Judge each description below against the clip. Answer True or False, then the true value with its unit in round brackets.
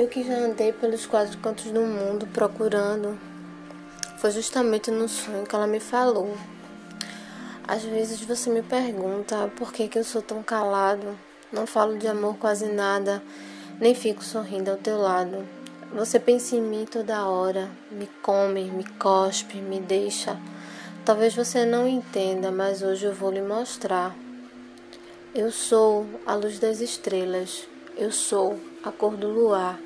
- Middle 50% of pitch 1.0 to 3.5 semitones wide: True (2.6 semitones)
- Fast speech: False (155 wpm)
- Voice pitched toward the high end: True (210 Hz)